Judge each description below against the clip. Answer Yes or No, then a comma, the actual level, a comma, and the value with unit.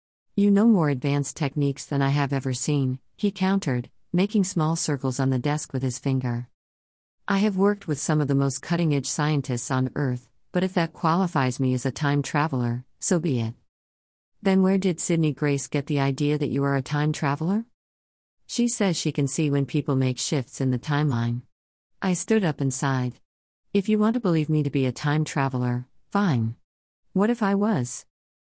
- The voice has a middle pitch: Yes, medium, 145 Hz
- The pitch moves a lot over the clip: No, average, 4.8 semitones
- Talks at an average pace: Yes, average, 195 wpm